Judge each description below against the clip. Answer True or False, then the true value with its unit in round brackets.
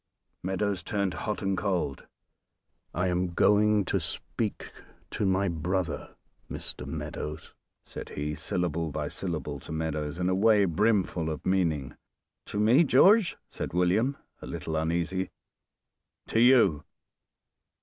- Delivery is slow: True (130 wpm)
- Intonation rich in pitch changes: False (4.3 semitones)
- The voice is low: True (90 Hz)